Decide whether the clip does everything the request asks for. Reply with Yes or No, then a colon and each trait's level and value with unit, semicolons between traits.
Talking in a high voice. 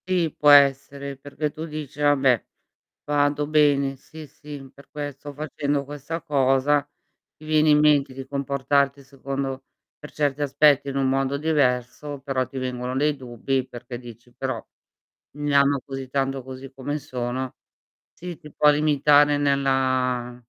No: medium, 140 Hz